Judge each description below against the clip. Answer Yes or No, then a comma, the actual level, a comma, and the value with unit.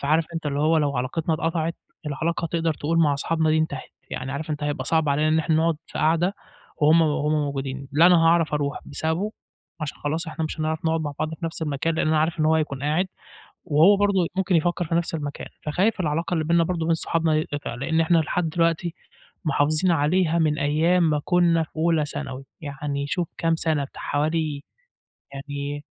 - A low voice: No, medium, 160 Hz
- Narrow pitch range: Yes, narrow, 2.2 semitones